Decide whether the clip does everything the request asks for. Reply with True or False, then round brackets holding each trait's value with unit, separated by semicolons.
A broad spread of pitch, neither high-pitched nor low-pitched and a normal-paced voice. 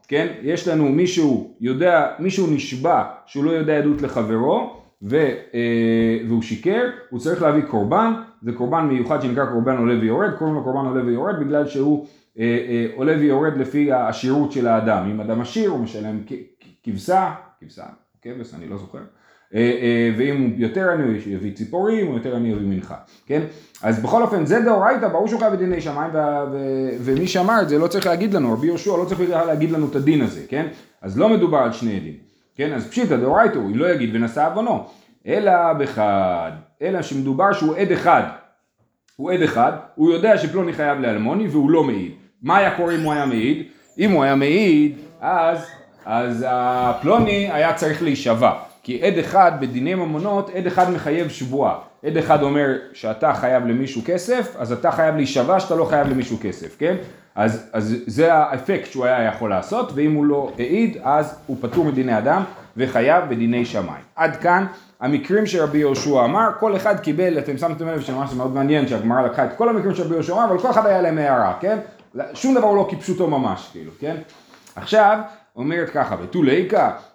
False (6.2 semitones; 150 Hz; 180 wpm)